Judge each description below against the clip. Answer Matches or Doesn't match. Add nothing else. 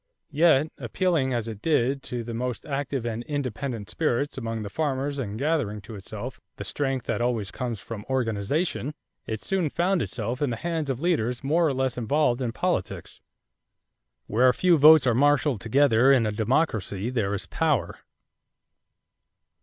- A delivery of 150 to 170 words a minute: Matches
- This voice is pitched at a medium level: Doesn't match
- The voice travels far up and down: Doesn't match